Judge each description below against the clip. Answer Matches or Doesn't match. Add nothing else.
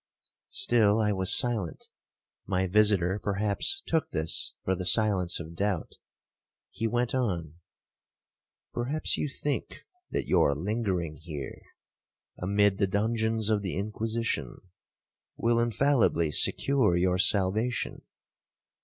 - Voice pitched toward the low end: Matches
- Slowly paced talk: Matches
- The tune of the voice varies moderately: Matches